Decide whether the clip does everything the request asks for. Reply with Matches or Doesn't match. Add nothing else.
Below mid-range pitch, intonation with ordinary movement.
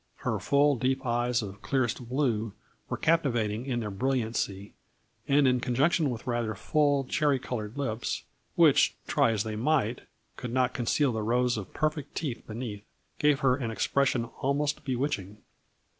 Matches